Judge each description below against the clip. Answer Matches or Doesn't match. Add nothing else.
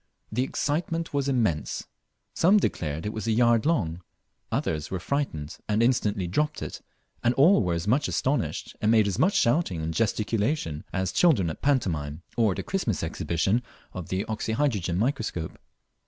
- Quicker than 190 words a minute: Doesn't match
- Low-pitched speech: Matches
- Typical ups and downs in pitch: Doesn't match